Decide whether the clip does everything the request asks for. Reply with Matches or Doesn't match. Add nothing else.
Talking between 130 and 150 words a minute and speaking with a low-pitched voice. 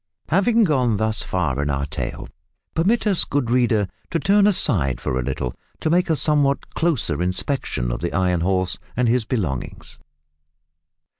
Doesn't match